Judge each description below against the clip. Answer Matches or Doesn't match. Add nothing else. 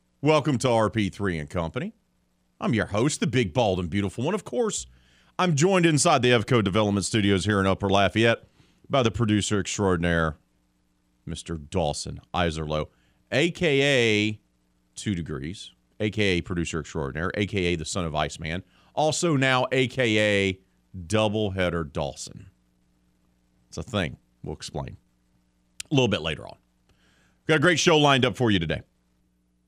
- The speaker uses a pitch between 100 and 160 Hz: Doesn't match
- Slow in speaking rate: Doesn't match